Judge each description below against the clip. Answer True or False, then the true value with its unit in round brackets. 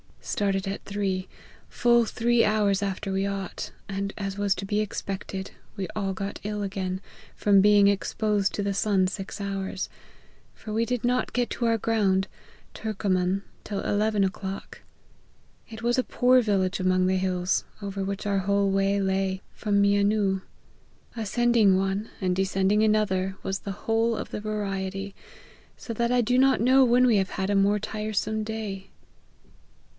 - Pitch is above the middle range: True (200 Hz)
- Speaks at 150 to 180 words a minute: True (160 wpm)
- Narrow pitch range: True (2.0 semitones)